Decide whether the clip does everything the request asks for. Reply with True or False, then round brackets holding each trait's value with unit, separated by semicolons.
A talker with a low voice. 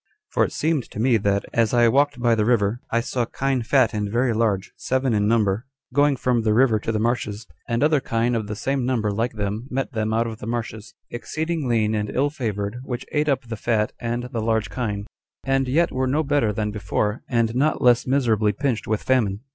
True (115 Hz)